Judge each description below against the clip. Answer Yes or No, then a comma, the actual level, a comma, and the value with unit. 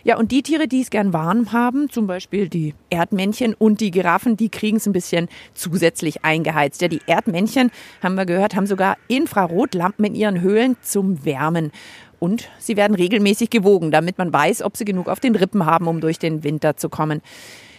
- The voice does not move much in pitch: No, average, 4.8 semitones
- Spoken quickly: Yes, fast, 195 wpm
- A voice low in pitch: No, high, 195 Hz